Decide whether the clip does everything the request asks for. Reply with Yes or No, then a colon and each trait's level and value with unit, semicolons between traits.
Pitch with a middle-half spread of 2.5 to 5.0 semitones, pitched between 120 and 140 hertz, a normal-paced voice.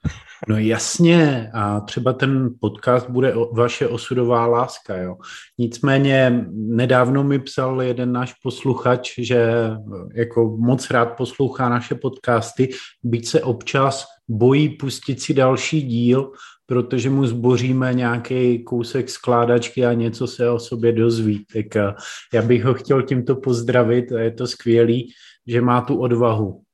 No: narrow, 1.8 semitones; low, 125 Hz; average, 135 wpm